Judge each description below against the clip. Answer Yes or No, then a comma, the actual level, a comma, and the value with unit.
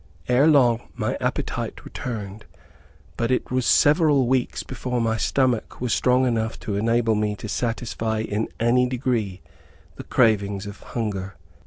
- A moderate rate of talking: Yes, average, 145 wpm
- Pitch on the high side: No, low, 115 Hz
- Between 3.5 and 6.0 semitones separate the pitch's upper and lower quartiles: No, average, 2.7 semitones